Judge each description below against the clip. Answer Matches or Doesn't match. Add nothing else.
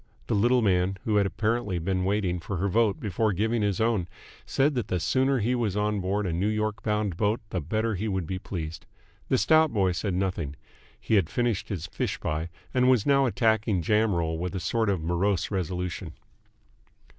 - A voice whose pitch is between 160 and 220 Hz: Doesn't match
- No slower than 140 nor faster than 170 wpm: Doesn't match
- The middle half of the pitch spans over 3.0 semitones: Matches